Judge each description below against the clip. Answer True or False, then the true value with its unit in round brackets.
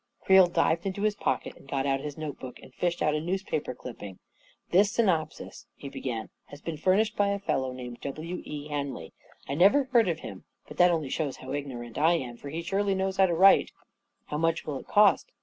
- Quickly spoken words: True (240 wpm)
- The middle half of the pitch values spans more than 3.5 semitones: True (5.6 semitones)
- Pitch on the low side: False (160 Hz)